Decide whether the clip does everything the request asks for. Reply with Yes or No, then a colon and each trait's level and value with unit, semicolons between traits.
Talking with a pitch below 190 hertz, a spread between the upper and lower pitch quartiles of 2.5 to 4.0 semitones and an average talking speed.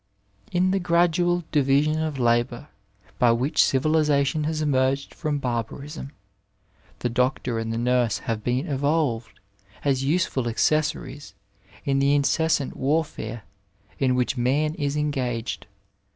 No: medium, 140 Hz; average, 3.6 semitones; slow, 125 wpm